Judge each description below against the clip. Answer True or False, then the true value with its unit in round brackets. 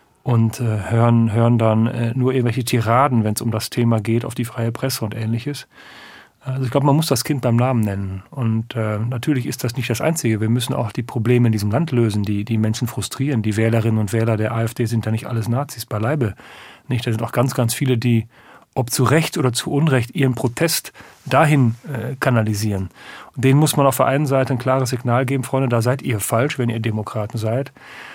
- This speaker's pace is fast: True (220 wpm)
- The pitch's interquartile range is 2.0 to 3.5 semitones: True (2.6 semitones)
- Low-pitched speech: True (120 Hz)